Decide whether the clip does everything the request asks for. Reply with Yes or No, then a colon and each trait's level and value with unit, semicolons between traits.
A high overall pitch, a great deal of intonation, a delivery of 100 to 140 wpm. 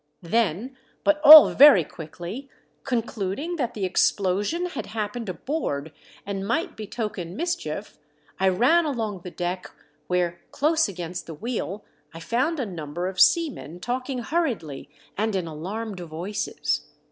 Yes: high, 205 Hz; wide, 6.6 semitones; slow, 135 wpm